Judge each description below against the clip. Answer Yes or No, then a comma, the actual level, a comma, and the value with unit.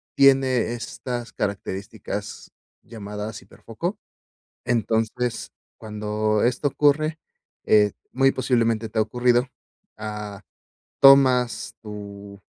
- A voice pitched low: Yes, low, 115 Hz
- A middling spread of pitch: Yes, average, 3.0 semitones